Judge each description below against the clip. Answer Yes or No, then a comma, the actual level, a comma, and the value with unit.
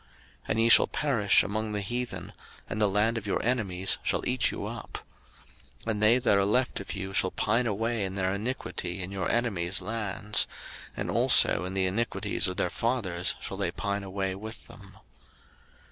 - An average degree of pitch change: Yes, average, 3.0 semitones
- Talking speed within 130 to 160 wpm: No, average, 190 wpm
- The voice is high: No, low, 100 Hz